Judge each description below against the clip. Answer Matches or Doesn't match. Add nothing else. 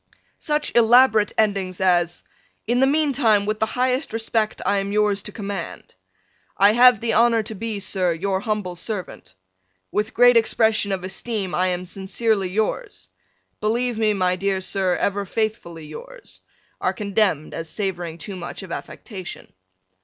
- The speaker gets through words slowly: Doesn't match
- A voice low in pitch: Doesn't match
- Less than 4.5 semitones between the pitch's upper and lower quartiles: Matches